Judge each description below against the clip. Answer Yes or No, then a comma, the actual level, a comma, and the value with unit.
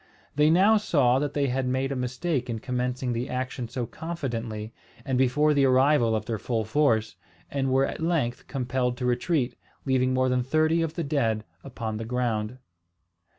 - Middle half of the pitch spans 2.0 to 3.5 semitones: Yes, average, 2.9 semitones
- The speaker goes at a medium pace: Yes, average, 180 wpm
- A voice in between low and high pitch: No, low, 130 Hz